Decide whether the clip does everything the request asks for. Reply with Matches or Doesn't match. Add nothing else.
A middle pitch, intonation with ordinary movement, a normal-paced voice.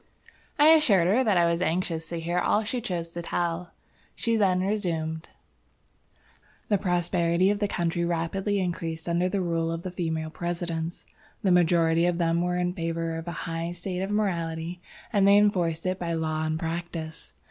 Doesn't match